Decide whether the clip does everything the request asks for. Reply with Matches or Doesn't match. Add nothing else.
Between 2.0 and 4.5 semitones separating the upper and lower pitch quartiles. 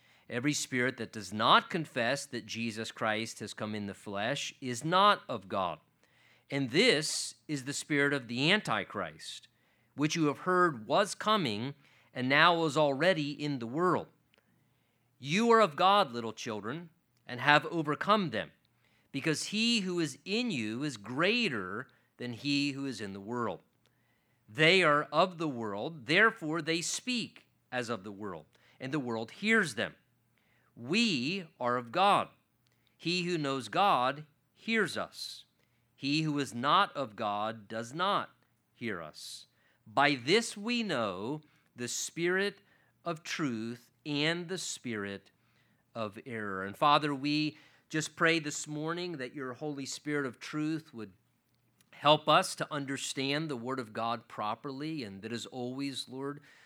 Doesn't match